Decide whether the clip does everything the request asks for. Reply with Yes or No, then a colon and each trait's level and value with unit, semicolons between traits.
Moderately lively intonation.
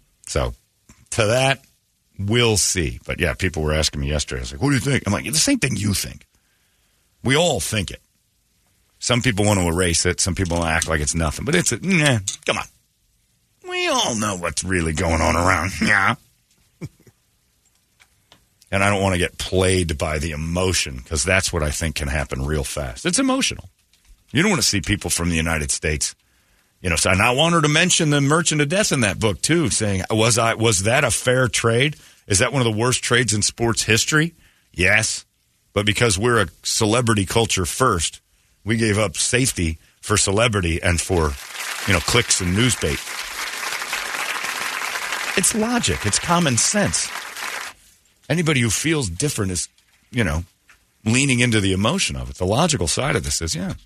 No: wide, 6.6 semitones